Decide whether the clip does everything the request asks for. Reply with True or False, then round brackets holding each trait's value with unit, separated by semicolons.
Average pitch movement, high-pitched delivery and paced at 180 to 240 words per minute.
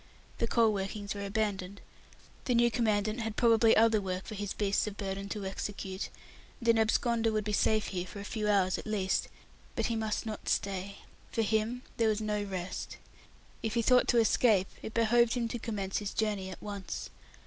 False (2.3 semitones; 215 Hz; 195 wpm)